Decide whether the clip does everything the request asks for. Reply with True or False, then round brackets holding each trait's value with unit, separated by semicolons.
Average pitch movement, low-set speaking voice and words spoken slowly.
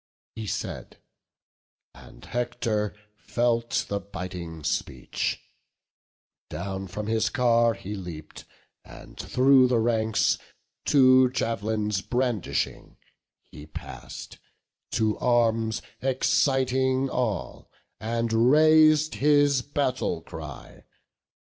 True (4.1 semitones; 115 Hz; 90 wpm)